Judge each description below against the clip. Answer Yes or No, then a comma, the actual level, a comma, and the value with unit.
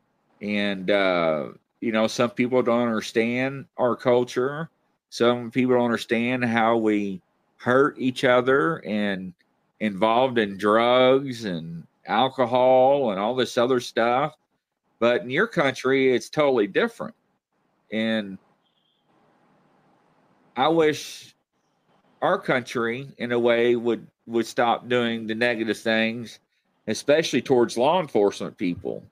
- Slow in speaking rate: Yes, slow, 115 wpm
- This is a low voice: Yes, low, 120 Hz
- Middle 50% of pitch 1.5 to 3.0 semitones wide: Yes, narrow, 2.5 semitones